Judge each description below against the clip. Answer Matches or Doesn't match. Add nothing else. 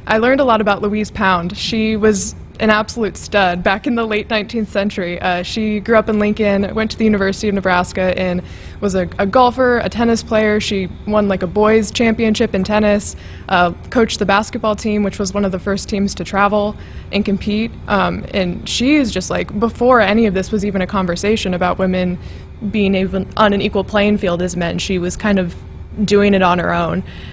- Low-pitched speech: Doesn't match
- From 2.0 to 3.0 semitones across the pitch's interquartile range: Matches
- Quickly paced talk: Matches